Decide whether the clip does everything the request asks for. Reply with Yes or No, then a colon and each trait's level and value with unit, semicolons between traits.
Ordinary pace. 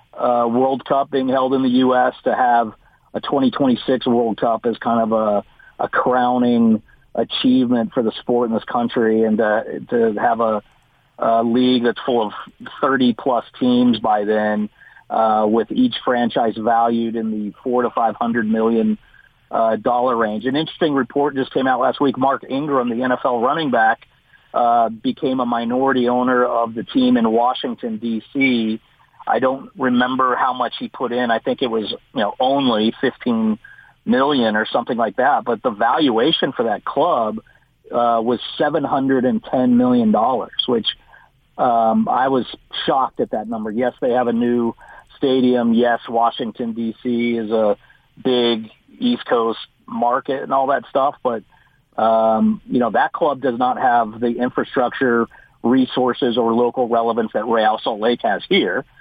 Yes: average, 170 wpm